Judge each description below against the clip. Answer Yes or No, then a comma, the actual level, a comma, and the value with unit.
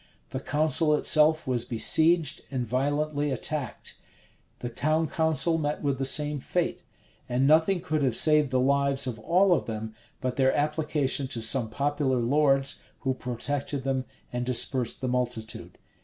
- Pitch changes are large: No, average, 3.1 semitones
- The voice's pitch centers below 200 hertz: Yes, medium, 140 Hz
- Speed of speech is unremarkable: Yes, average, 155 wpm